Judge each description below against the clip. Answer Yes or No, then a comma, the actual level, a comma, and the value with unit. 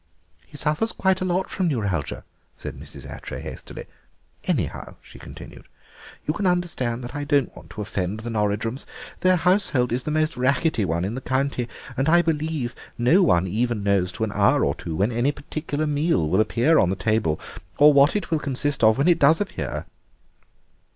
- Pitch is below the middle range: Yes, low, 130 Hz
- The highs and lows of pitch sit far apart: Yes, wide, 6.3 semitones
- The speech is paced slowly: No, average, 190 wpm